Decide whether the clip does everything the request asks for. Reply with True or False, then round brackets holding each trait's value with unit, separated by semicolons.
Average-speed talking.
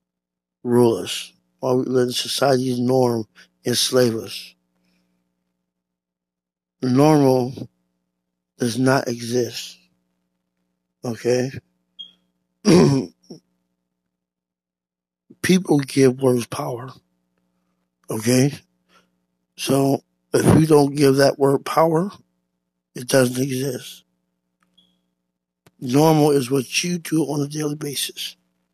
False (80 wpm)